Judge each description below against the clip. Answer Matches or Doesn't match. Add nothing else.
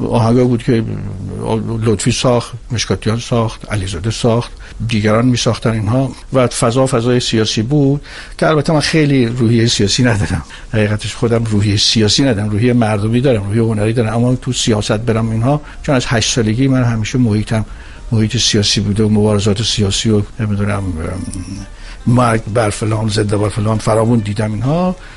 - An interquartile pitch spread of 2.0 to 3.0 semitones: Matches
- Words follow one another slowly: Doesn't match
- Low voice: Matches